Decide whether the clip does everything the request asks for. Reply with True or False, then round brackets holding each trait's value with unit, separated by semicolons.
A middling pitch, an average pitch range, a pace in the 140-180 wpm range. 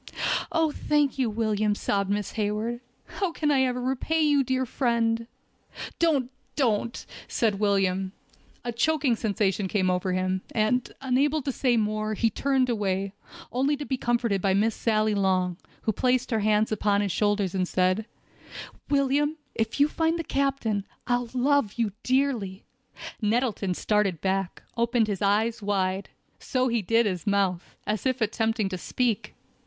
False (225 Hz; 4.3 semitones; 155 wpm)